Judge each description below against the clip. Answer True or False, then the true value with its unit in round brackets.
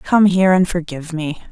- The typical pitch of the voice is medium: True (175 Hz)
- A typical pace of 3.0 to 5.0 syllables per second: False (5.8 syllables/s)